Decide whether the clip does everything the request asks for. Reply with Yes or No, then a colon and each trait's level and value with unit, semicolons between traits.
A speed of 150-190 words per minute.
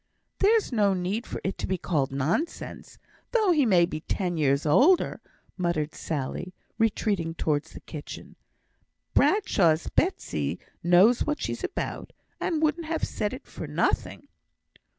No: average, 140 wpm